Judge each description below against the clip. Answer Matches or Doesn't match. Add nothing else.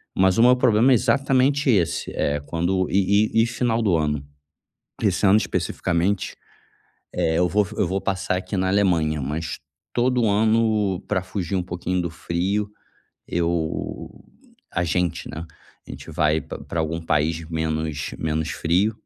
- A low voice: Matches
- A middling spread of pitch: Matches